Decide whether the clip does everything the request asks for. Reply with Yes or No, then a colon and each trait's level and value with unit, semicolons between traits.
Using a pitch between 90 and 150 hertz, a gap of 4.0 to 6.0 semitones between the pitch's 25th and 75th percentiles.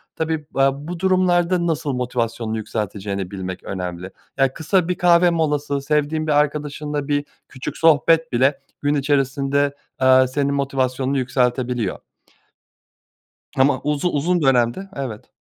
No: medium, 140 Hz; average, 3.6 semitones